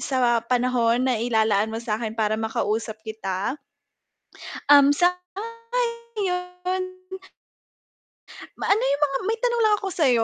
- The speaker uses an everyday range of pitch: No, wide, 8.6 semitones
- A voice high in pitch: Yes, very high, 255 Hz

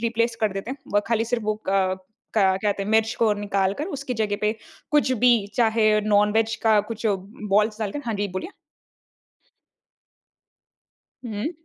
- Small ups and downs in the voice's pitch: Yes, narrow, 2.1 semitones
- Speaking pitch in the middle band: No, high, 215 Hz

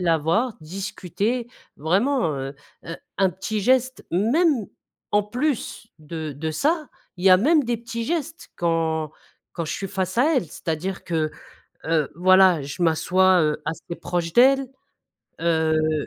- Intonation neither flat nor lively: No, wide, 6.4 semitones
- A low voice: No, medium, 185 Hz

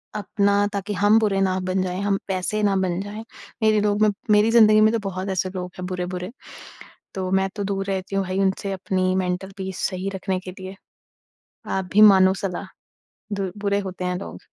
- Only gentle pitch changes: Yes, narrow, 1.7 semitones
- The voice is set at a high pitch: Yes, high, 195 Hz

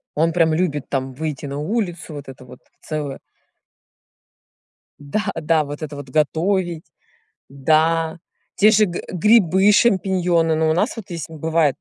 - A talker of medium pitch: Yes, medium, 160 Hz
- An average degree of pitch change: Yes, average, 3.6 semitones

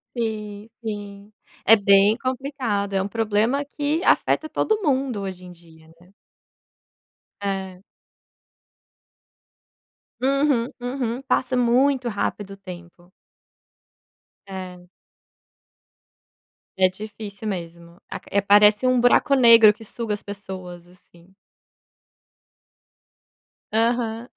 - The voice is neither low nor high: No, high, 210 Hz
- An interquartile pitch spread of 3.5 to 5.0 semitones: Yes, average, 4.4 semitones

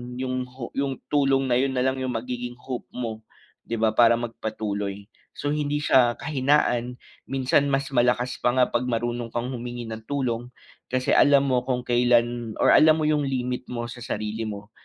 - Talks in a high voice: No, low, 125 Hz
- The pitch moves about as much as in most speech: No, narrow, 2.0 semitones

